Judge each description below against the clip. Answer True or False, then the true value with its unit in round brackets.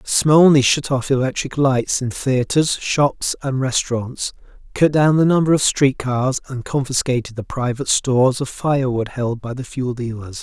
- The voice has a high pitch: False (130 Hz)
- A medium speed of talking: True (180 wpm)